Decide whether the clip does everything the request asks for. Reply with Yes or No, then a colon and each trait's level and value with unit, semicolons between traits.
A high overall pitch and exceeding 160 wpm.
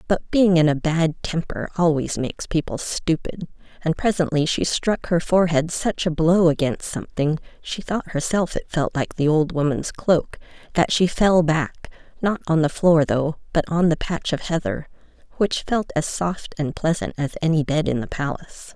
No: medium, 165 Hz; average, 175 wpm